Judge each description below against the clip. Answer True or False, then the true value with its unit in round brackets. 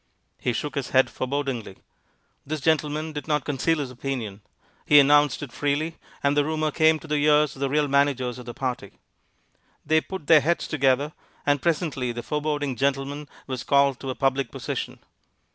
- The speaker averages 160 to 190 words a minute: True (180 wpm)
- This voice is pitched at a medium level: True (145 Hz)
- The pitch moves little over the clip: True (2.3 semitones)